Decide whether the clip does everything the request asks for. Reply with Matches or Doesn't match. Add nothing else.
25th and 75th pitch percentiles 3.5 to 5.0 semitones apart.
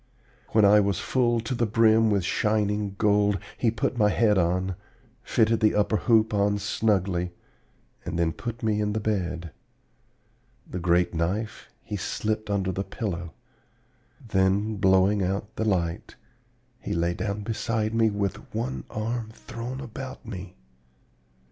Doesn't match